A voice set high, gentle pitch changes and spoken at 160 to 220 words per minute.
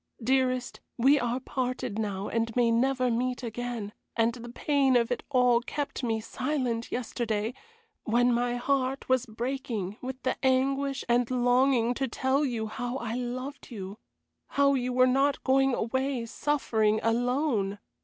No: high, 245 Hz; narrow, 2.3 semitones; average, 150 wpm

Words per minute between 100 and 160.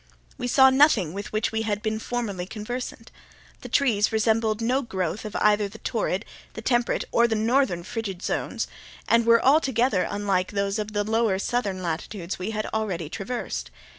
No: average, 170 wpm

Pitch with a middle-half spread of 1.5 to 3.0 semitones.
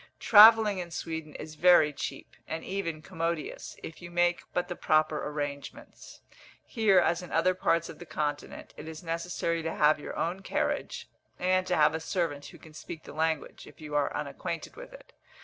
Yes: narrow, 2.6 semitones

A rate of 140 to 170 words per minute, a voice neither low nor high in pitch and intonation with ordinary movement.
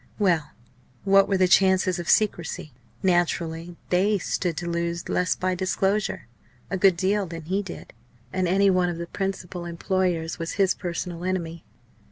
No: average, 160 wpm; medium, 180 Hz; narrow, 2.0 semitones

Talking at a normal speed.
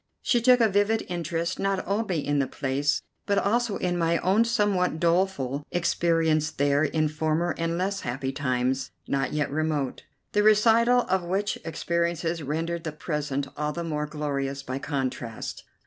Yes: average, 160 wpm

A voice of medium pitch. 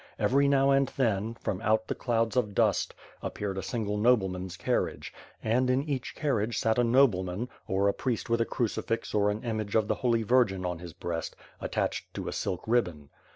No: low, 110 Hz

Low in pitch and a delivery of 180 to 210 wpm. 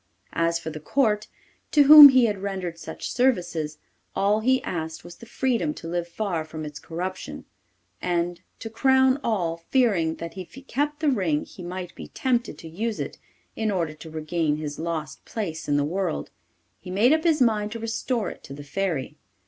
No: medium, 185 Hz; average, 190 wpm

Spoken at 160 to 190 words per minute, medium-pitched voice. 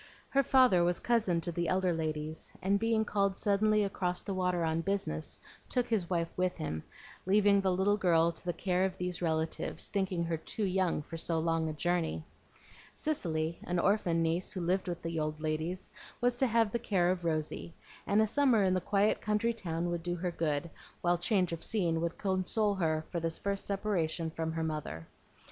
No: average, 200 wpm; medium, 180 Hz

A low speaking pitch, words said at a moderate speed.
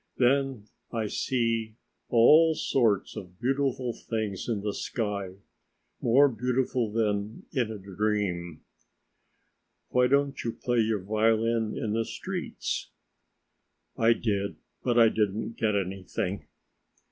No: low, 115 Hz; slow, 115 wpm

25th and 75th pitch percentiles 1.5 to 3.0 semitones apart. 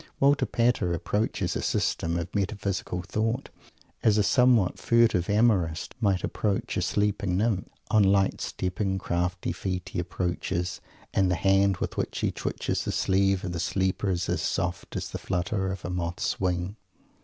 Yes: narrow, 2.6 semitones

